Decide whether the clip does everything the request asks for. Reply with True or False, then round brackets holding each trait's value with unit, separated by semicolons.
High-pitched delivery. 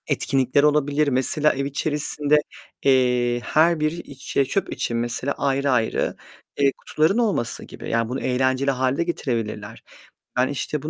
False (135 Hz)